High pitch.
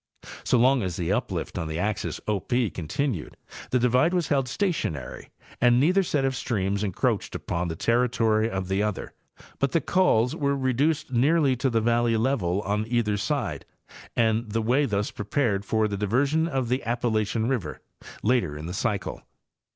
No: low, 115 Hz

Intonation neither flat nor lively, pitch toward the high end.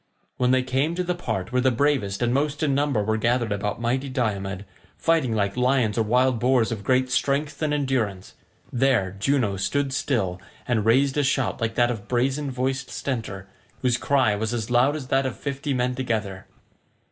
No: average, 3.7 semitones; low, 125 Hz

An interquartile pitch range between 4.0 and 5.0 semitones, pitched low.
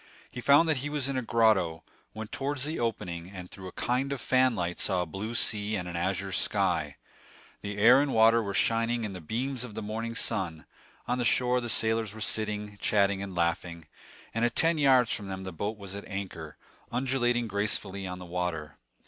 Yes: average, 4.3 semitones; low, 110 Hz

